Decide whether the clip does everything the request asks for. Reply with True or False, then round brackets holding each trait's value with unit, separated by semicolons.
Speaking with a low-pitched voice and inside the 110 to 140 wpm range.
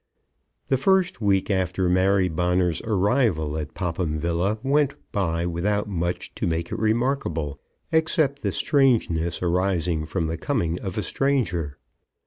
True (90 Hz; 135 wpm)